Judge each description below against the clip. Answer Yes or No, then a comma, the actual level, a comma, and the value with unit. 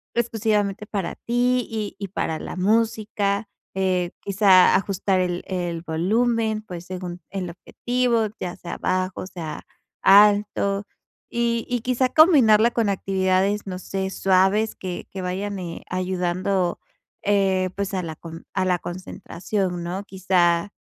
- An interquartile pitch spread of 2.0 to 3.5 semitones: Yes, average, 2.8 semitones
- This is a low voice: No, high, 195 Hz